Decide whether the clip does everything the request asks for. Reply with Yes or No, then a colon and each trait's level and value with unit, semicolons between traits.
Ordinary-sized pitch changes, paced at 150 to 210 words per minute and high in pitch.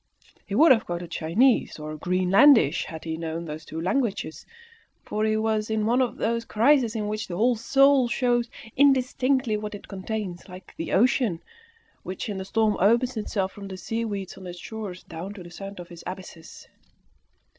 Yes: average, 4.5 semitones; average, 180 wpm; high, 210 Hz